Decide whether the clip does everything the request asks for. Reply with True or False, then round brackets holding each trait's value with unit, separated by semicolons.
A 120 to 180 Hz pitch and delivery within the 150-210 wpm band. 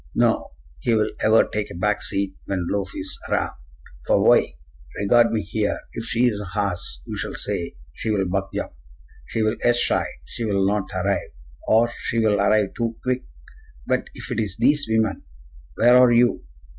False (105 Hz; 185 wpm)